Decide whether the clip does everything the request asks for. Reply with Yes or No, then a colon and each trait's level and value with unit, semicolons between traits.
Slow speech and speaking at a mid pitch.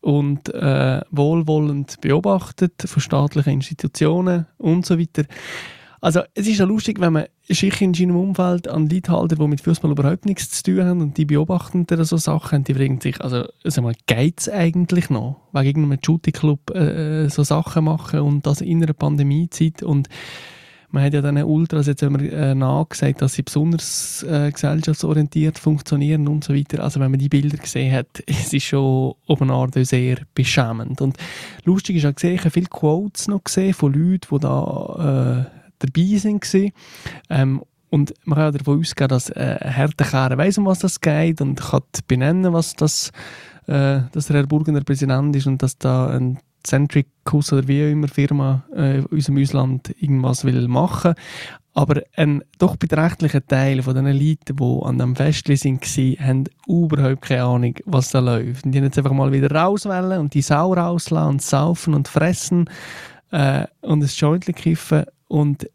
No: average, 185 wpm; medium, 150 Hz